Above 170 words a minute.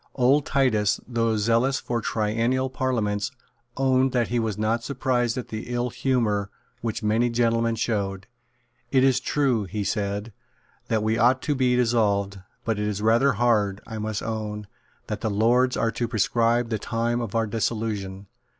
No: average, 165 wpm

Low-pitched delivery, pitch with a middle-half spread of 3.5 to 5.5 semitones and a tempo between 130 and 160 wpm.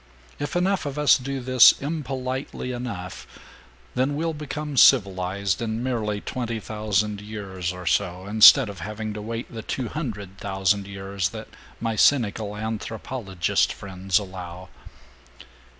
Yes: low, 110 Hz; average, 4.8 semitones; slow, 135 wpm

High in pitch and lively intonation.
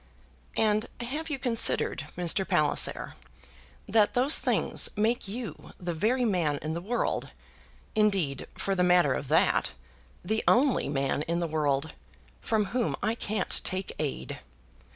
Yes: high, 195 Hz; wide, 6.2 semitones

